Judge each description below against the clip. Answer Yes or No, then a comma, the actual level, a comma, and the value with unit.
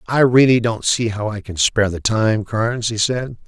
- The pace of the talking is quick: Yes, fast, 225 wpm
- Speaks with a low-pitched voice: Yes, low, 115 Hz